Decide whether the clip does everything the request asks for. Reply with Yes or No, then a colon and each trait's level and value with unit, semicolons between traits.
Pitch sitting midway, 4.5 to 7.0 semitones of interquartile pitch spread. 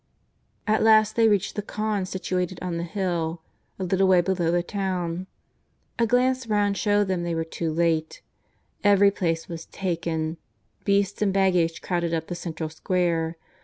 No: medium, 180 Hz; average, 3.2 semitones